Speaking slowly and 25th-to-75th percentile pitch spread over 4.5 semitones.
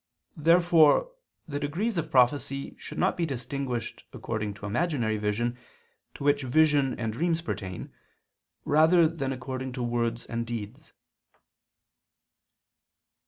Yes: slow, 120 wpm; average, 5.1 semitones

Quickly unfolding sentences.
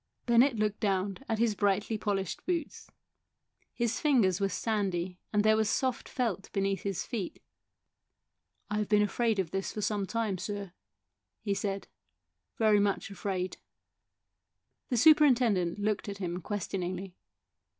No: average, 145 wpm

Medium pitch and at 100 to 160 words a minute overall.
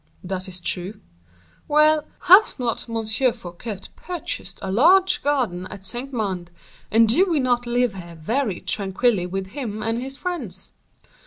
No: high, 225 Hz; average, 150 wpm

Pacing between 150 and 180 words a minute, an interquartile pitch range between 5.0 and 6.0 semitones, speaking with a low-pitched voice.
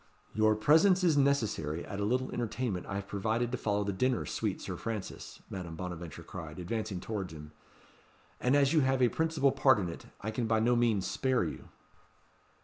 No: average, 190 wpm; average, 5.3 semitones; low, 110 Hz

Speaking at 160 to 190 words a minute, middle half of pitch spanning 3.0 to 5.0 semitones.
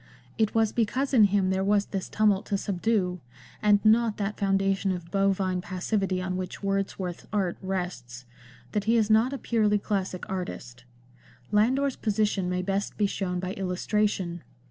No: average, 165 wpm; narrow, 2.5 semitones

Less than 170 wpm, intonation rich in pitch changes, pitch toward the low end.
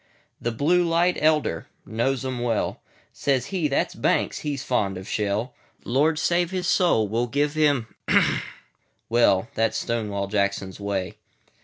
Yes: average, 150 wpm; wide, 6.0 semitones; low, 120 Hz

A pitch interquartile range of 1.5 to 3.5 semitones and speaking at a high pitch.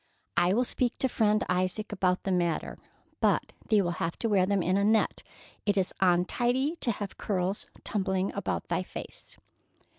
Yes: average, 2.9 semitones; high, 195 Hz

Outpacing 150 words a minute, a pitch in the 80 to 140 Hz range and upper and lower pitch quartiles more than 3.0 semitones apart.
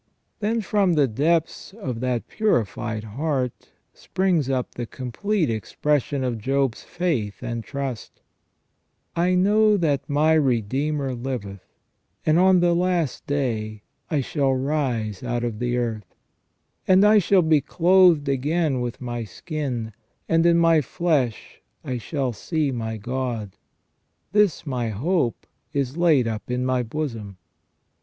No: slow, 135 wpm; low, 135 Hz; wide, 5.6 semitones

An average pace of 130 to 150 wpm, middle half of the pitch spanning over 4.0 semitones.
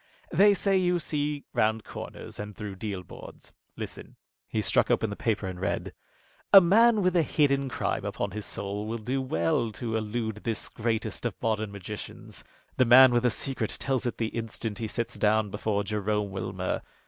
No: average, 185 wpm; average, 4.4 semitones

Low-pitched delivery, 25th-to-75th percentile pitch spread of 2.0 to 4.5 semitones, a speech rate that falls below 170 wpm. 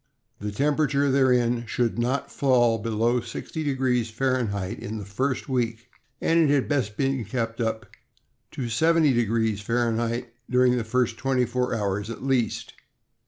Yes: low, 120 Hz; average, 2.7 semitones; average, 140 wpm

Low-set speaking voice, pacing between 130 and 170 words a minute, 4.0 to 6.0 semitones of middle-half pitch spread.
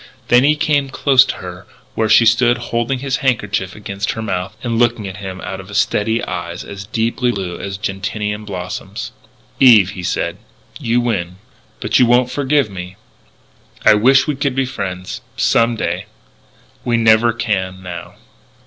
Yes: low, 110 Hz; average, 165 wpm; average, 4.3 semitones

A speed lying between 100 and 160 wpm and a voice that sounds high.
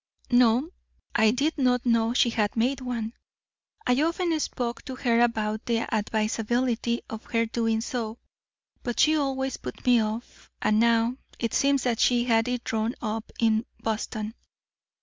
Yes: average, 155 wpm; high, 235 Hz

